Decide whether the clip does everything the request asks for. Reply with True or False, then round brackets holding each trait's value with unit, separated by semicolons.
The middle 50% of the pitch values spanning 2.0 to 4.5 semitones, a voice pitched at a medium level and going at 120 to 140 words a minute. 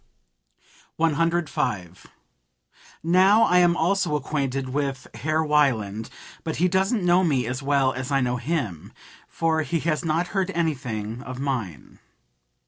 False (5.0 semitones; 150 Hz; 135 wpm)